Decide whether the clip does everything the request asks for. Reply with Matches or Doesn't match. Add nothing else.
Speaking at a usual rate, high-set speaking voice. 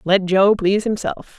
Matches